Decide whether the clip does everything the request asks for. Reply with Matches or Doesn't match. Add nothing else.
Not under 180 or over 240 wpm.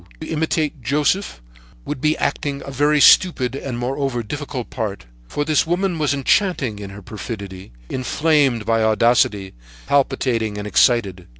Doesn't match